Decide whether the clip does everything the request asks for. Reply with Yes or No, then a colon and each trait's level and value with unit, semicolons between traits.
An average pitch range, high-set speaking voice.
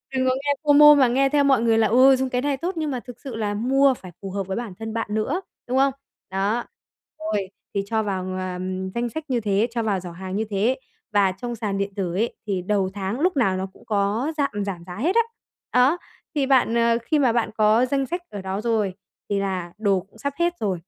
Yes: average, 5.0 semitones; high, 225 Hz